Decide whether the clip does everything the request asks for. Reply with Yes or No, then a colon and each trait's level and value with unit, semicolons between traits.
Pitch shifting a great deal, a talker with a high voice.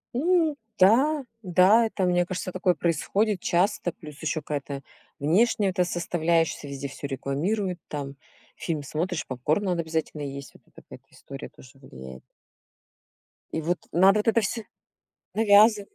No: wide, 5.7 semitones; medium, 175 Hz